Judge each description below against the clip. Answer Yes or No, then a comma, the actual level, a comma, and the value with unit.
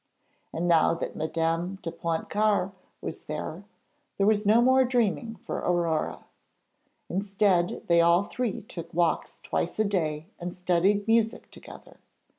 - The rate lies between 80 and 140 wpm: Yes, slow, 135 wpm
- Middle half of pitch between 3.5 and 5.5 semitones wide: Yes, average, 3.8 semitones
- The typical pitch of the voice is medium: Yes, medium, 180 Hz